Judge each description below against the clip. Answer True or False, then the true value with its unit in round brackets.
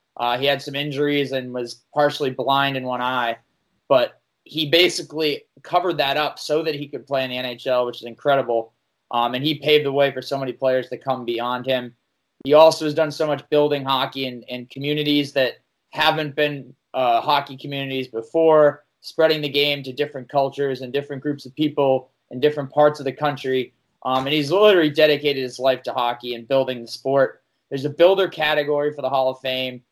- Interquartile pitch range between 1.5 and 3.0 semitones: True (2.5 semitones)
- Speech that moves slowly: False (200 wpm)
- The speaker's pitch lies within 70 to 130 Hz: False (140 Hz)